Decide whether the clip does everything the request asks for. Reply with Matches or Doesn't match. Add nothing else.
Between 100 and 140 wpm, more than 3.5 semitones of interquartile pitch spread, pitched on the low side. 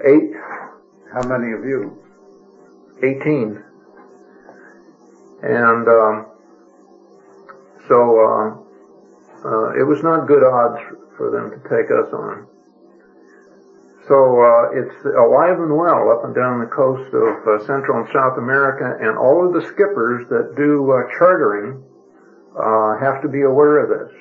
Matches